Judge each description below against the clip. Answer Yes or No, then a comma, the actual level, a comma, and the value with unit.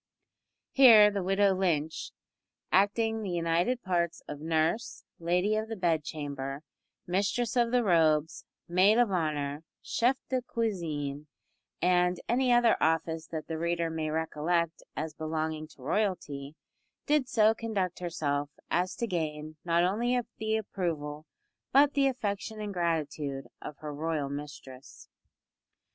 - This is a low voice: No, medium, 170 Hz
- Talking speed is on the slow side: Yes, slow, 130 wpm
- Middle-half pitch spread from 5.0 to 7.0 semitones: Yes, wide, 5.6 semitones